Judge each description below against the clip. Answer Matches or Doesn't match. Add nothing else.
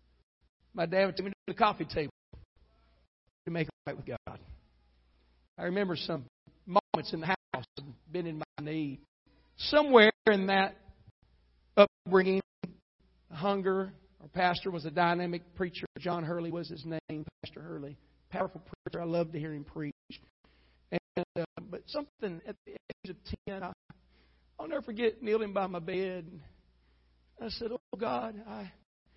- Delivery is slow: Doesn't match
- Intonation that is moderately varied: Doesn't match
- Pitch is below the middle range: Doesn't match